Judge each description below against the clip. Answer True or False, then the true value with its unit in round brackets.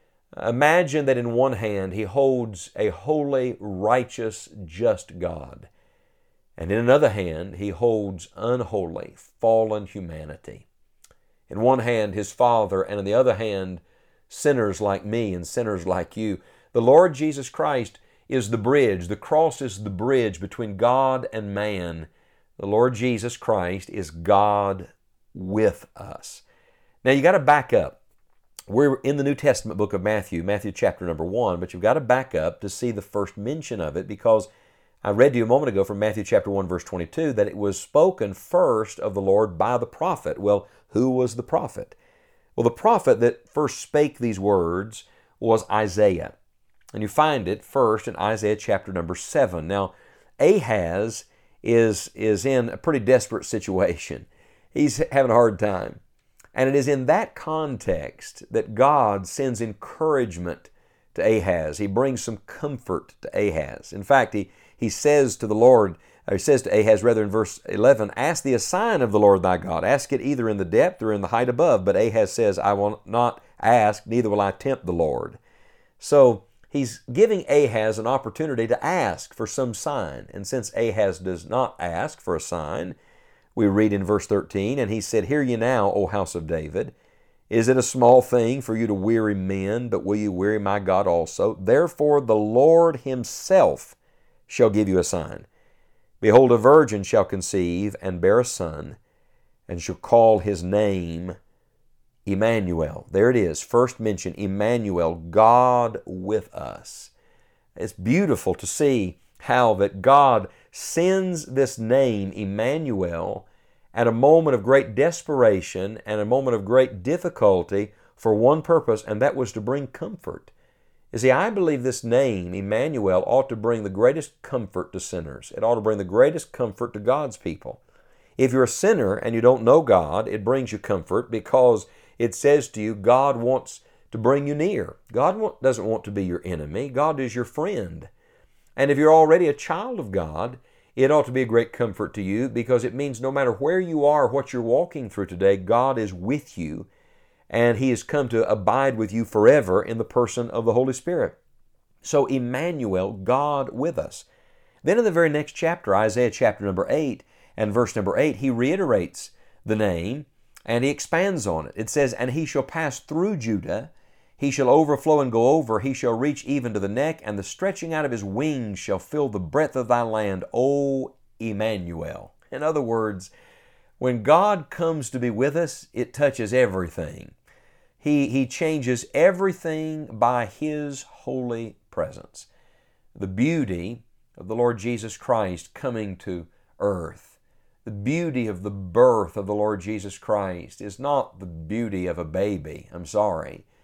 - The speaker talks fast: False (175 wpm)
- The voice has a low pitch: True (115 Hz)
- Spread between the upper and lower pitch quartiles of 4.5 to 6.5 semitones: True (5.0 semitones)